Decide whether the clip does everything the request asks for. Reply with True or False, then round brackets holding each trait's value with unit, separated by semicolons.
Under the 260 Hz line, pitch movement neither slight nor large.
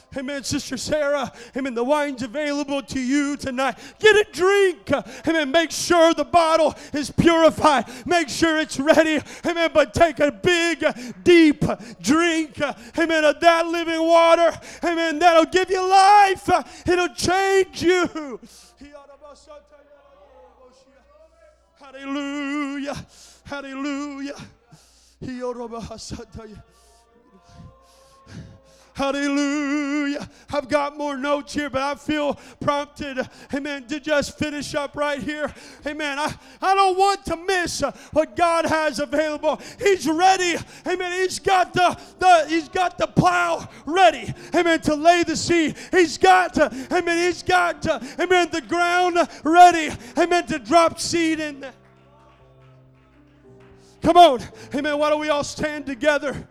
False (300 Hz; 3.2 semitones)